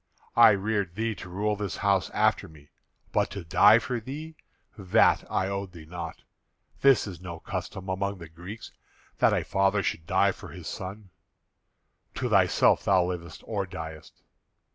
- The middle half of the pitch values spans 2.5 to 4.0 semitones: Yes, average, 3.1 semitones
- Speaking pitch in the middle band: No, very low, 95 Hz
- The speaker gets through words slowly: No, average, 165 wpm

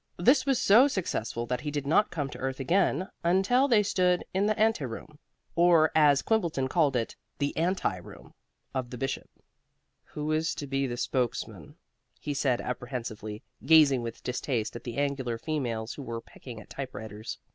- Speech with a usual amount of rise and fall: No, wide, 5.9 semitones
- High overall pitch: No, medium, 140 Hz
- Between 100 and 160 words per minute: No, average, 170 wpm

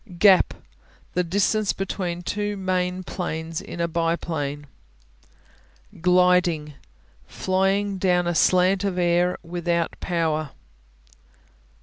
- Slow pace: Yes, slow, 95 wpm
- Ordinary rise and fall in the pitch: No, narrow, 1.8 semitones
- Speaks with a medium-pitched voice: Yes, medium, 180 Hz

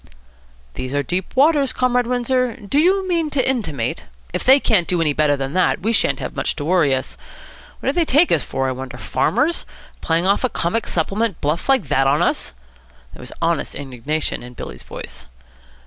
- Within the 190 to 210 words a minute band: Yes, average, 200 wpm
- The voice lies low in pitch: No, medium, 185 Hz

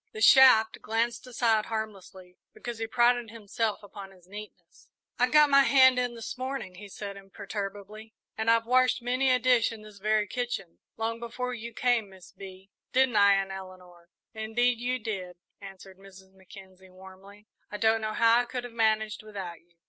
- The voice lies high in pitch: Yes, high, 220 Hz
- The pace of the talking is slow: No, average, 180 wpm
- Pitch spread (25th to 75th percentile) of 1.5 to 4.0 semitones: Yes, average, 3.5 semitones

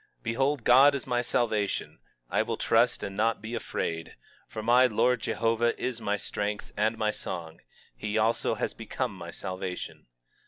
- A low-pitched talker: Yes, low, 110 Hz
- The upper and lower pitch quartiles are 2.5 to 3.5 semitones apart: Yes, average, 2.9 semitones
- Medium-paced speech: Yes, average, 165 wpm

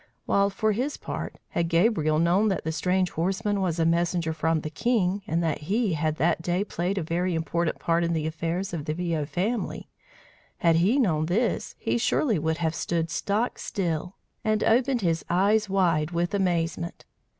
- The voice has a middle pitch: Yes, medium, 175 Hz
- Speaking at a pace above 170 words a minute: Yes, average, 185 wpm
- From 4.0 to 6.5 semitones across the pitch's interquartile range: No, average, 3.5 semitones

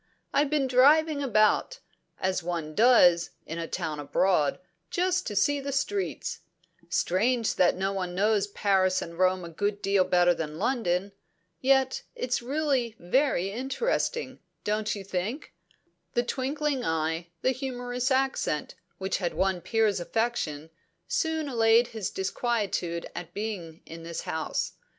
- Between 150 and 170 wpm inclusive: No, slow, 135 wpm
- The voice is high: Yes, high, 210 Hz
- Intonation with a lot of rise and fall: Yes, wide, 6.6 semitones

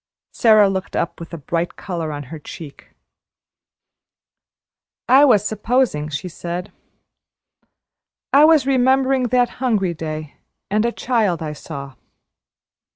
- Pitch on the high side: Yes, high, 195 Hz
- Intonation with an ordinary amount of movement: No, wide, 7.6 semitones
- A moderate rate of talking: No, slow, 120 wpm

